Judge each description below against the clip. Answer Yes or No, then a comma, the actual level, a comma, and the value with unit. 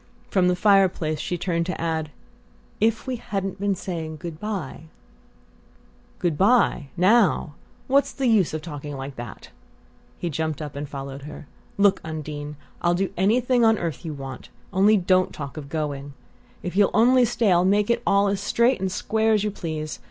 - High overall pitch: No, medium, 180 Hz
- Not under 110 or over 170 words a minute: No, average, 180 wpm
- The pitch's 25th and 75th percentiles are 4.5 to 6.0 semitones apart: Yes, average, 5.0 semitones